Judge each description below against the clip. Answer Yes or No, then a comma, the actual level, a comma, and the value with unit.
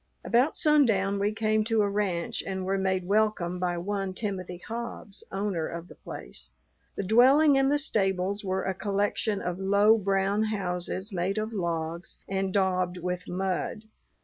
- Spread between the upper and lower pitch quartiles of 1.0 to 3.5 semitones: Yes, average, 2.8 semitones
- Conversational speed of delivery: Yes, average, 160 wpm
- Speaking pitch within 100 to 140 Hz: No, high, 195 Hz